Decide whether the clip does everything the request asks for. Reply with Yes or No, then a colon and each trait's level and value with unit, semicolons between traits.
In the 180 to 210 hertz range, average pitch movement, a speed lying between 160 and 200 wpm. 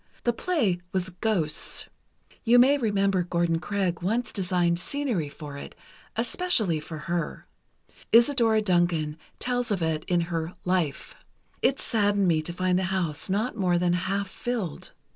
No: medium, 185 Hz; average, 4.4 semitones; average, 145 wpm